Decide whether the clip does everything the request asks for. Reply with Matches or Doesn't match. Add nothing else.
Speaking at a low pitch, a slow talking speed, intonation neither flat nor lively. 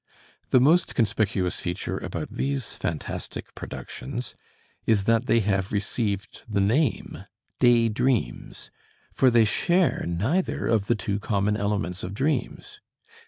Matches